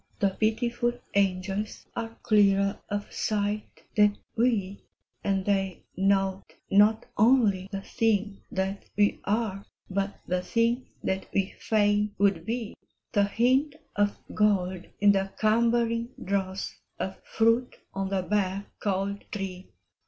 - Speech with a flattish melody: Yes, narrow, 2.3 semitones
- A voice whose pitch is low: No, high, 205 Hz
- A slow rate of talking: Yes, slow, 125 wpm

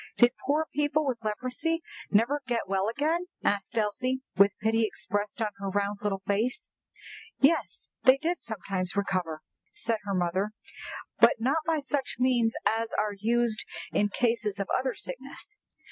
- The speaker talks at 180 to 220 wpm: No, average, 150 wpm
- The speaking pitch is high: Yes, high, 225 Hz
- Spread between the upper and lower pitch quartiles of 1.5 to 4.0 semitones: No, average, 4.6 semitones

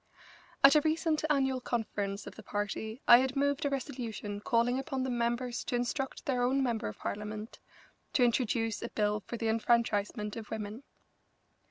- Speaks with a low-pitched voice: No, high, 240 Hz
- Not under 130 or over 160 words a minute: No, average, 170 wpm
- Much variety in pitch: No, average, 3.5 semitones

